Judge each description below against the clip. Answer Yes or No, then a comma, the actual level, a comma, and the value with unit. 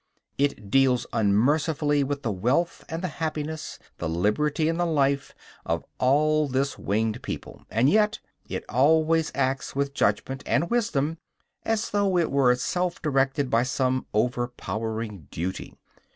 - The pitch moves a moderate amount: Yes, average, 4.3 semitones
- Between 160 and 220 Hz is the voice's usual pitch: No, medium, 140 Hz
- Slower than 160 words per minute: Yes, average, 140 wpm